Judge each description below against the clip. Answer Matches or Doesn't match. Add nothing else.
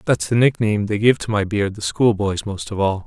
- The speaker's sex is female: Doesn't match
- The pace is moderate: Doesn't match